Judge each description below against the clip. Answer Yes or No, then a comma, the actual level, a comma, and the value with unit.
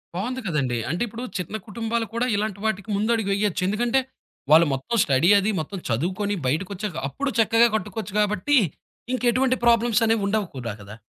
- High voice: Yes, high, 210 Hz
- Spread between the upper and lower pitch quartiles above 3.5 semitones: Yes, average, 4.4 semitones